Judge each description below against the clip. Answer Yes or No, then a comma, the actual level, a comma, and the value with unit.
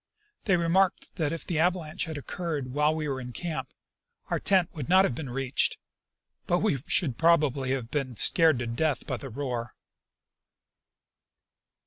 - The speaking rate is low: No, average, 165 wpm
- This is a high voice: No, medium, 150 Hz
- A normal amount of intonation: Yes, average, 4.4 semitones